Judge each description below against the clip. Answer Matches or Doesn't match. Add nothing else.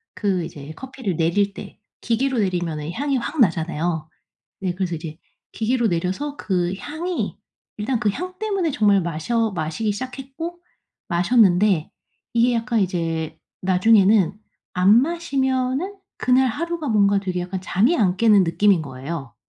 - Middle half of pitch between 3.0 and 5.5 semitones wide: Doesn't match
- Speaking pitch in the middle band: Doesn't match